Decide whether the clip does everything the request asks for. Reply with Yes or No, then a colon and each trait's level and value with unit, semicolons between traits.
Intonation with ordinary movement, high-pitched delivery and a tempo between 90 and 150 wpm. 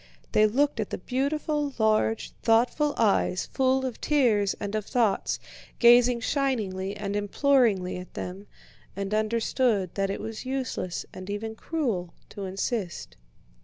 Yes: average, 4.5 semitones; high, 220 Hz; slow, 135 wpm